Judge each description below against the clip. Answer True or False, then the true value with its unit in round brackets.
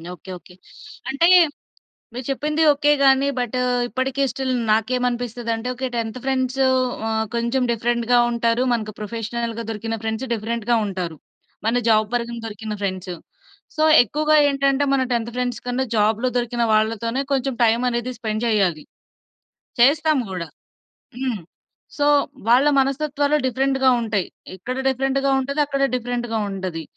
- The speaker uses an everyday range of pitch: True (3.2 semitones)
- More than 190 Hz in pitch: True (240 Hz)